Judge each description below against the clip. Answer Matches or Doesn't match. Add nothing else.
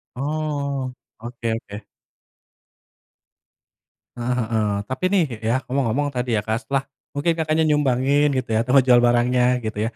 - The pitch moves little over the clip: Doesn't match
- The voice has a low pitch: Matches